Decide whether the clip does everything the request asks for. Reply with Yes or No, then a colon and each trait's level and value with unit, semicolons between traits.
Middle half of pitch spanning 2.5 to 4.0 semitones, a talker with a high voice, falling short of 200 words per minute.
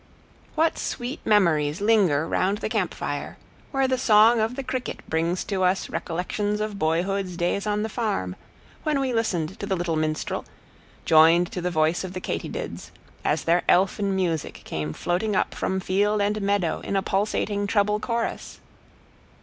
Yes: average, 3.6 semitones; high, 195 Hz; average, 165 wpm